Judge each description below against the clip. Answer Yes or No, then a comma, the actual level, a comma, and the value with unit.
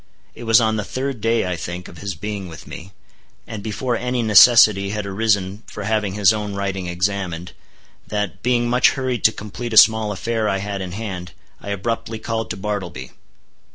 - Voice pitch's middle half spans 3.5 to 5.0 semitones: No, average, 2.8 semitones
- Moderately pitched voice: No, low, 105 Hz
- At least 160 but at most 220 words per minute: Yes, average, 190 wpm